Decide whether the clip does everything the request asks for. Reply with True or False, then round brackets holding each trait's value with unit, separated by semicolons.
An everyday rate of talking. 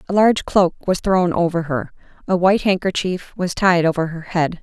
True (195 wpm)